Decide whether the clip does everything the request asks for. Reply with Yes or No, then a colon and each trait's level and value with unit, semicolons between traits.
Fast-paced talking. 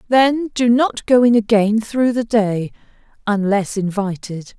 No: average, 145 wpm